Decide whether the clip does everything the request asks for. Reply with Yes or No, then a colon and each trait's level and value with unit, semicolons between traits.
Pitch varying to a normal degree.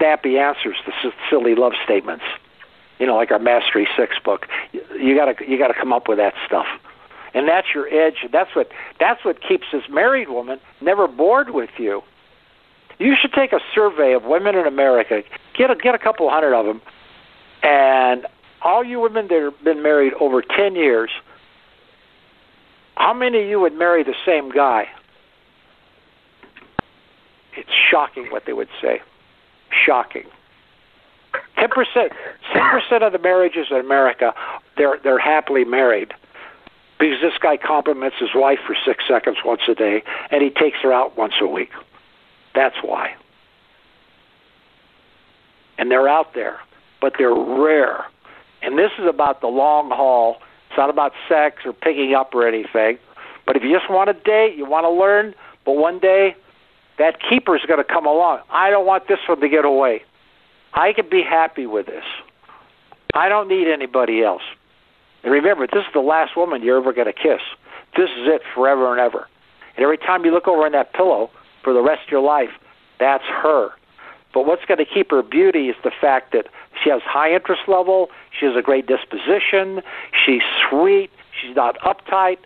No: wide, 8.1 semitones